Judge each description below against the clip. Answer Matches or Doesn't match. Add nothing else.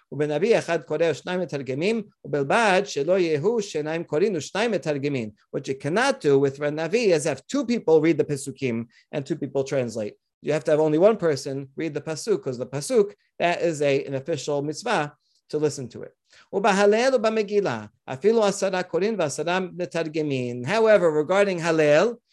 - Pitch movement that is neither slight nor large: Doesn't match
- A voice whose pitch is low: Doesn't match